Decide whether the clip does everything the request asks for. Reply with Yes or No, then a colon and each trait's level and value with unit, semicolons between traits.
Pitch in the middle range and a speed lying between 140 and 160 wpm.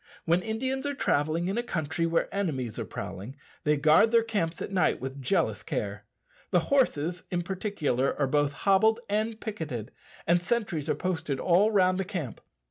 No: medium, 175 Hz; average, 175 wpm